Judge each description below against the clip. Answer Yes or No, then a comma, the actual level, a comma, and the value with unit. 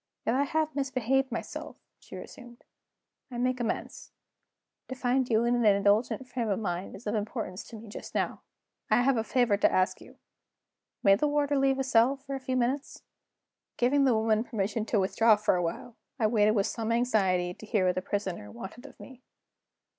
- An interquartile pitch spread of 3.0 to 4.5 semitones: Yes, average, 3.9 semitones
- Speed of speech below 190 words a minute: No, average, 200 wpm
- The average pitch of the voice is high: Yes, high, 230 Hz